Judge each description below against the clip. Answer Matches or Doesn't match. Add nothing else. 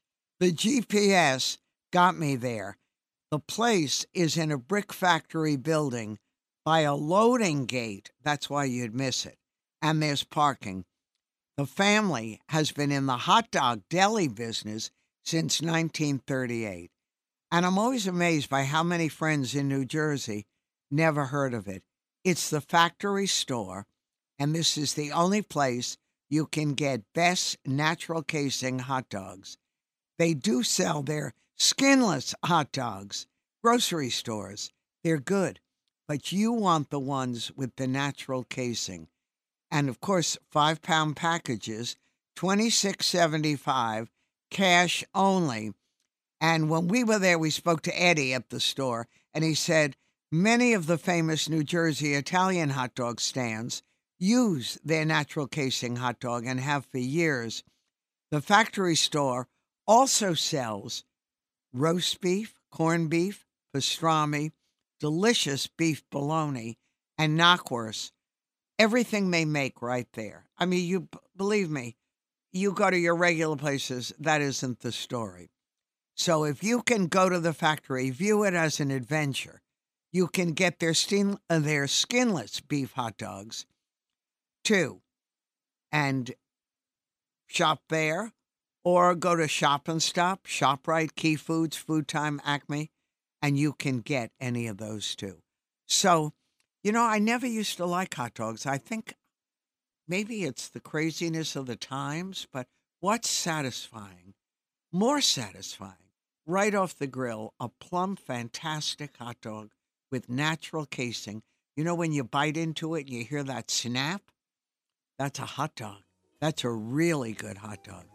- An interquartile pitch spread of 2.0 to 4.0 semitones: Doesn't match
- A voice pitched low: Doesn't match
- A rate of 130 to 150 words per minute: Matches